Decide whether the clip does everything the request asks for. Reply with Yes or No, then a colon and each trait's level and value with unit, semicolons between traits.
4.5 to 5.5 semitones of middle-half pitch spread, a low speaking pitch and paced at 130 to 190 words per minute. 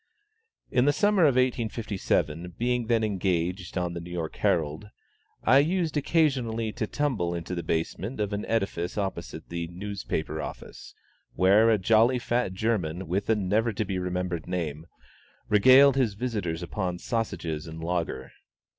Yes: average, 5.2 semitones; low, 100 Hz; average, 150 wpm